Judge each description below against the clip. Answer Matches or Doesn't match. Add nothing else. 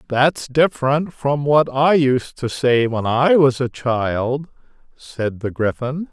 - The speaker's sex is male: Matches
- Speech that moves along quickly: Doesn't match